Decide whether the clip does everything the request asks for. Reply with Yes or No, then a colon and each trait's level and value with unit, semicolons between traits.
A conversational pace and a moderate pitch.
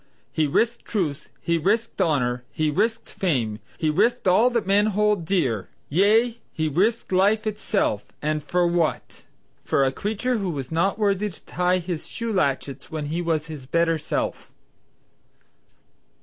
Yes: average, 155 wpm; medium, 175 Hz